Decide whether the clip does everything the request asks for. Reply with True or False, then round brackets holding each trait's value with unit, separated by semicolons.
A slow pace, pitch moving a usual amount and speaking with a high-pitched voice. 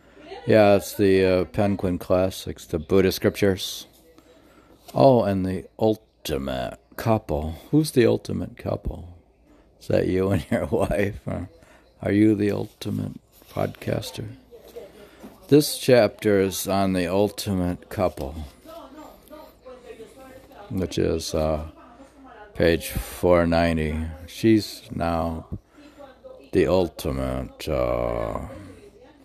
False (95 wpm; 4.6 semitones; 100 Hz)